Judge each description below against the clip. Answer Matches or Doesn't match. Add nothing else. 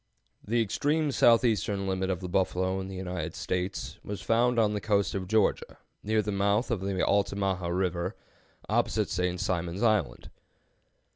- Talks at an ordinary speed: Matches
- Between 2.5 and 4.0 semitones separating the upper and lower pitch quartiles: Matches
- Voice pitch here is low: Matches